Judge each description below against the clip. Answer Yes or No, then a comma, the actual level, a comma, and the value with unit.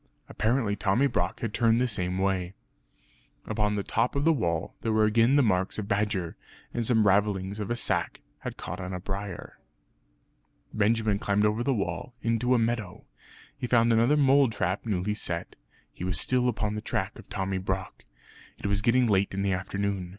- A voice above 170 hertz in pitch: No, low, 105 Hz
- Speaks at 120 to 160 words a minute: No, average, 185 wpm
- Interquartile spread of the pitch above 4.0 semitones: No, average, 3.4 semitones